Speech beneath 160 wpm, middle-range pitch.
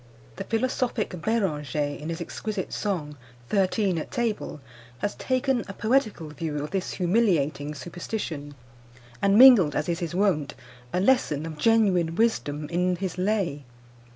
Yes: average, 140 wpm; medium, 180 Hz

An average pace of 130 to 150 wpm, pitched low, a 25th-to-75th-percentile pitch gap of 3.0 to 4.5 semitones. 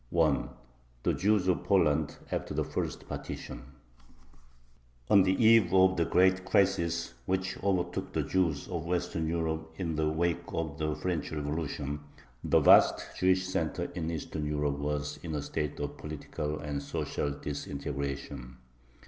Yes: average, 140 wpm; very low, 80 Hz; average, 3.7 semitones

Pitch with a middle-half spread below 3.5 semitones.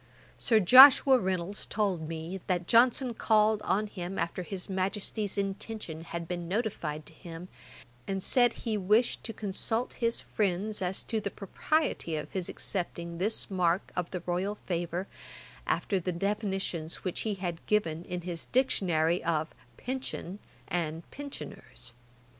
No: average, 3.8 semitones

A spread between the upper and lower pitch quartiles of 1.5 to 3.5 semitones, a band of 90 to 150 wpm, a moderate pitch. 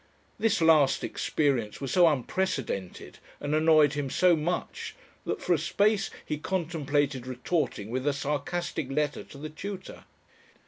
No: average, 4.0 semitones; average, 140 wpm; medium, 150 Hz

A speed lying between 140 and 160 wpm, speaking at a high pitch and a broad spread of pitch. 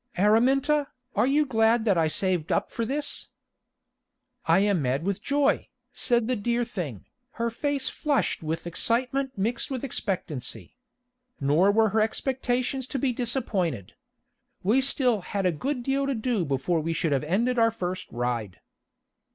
Yes: average, 155 wpm; high, 225 Hz; wide, 6.7 semitones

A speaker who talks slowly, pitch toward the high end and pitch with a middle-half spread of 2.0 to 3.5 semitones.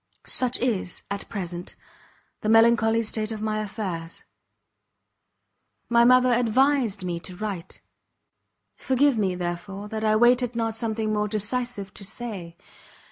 Yes: slow, 130 wpm; high, 215 Hz; average, 3.2 semitones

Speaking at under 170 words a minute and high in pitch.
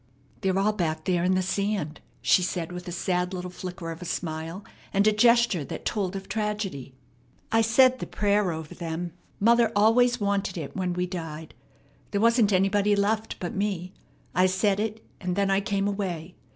No: average, 185 wpm; high, 195 Hz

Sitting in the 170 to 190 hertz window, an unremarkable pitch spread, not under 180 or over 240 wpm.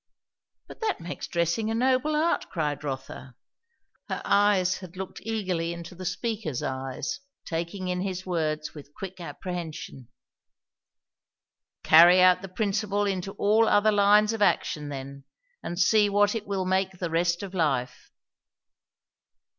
No: medium, 185 Hz; average, 3.7 semitones; average, 140 wpm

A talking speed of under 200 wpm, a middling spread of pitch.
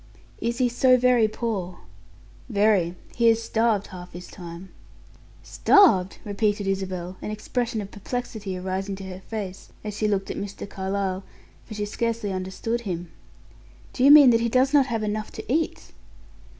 Yes: average, 165 wpm; average, 3.6 semitones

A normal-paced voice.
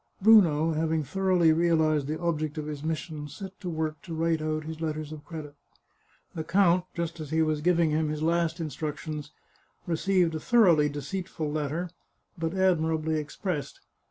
Yes: average, 165 wpm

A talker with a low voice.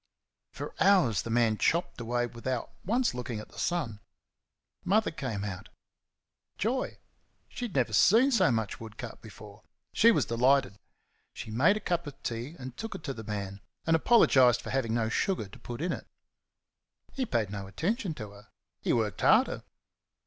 Yes: low, 125 Hz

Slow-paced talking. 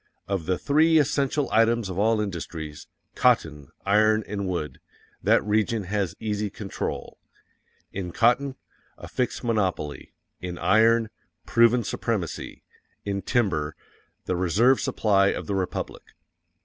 Yes: slow, 125 wpm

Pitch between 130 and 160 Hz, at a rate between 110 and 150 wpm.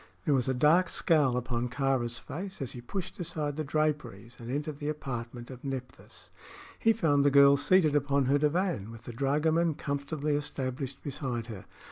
No: medium, 140 Hz; average, 175 wpm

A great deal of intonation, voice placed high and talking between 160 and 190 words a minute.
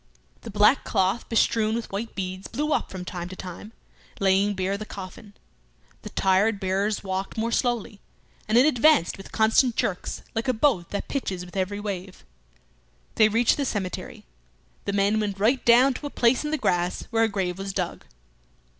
No: average, 3.3 semitones; high, 205 Hz; average, 180 wpm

